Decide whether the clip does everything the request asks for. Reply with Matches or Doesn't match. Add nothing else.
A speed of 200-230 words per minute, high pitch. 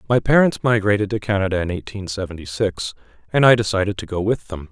Doesn't match